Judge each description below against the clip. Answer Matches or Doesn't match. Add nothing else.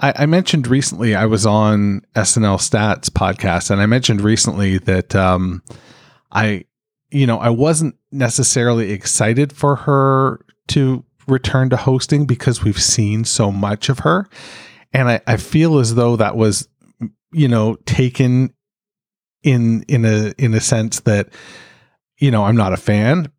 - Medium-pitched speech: Doesn't match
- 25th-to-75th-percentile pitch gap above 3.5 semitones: Matches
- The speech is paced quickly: Doesn't match